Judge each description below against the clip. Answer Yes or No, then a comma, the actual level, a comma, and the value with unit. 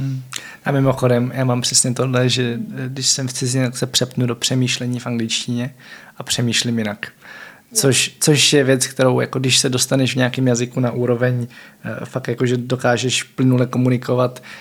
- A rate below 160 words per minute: No, average, 165 wpm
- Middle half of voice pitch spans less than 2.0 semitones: Yes, narrow, 1.2 semitones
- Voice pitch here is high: No, low, 125 Hz